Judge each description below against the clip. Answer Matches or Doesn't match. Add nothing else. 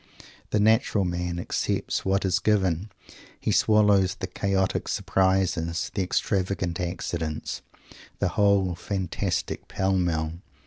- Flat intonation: Matches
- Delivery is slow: Matches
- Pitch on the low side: Matches